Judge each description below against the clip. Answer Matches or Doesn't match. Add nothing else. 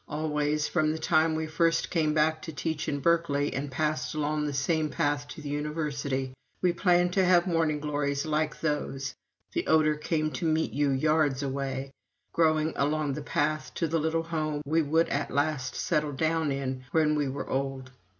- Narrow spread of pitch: Matches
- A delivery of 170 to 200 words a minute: Matches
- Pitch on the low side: Doesn't match